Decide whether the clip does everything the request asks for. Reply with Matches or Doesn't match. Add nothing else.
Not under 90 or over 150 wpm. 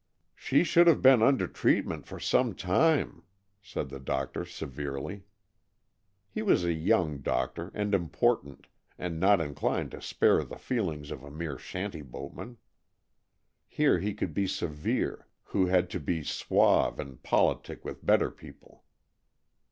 Matches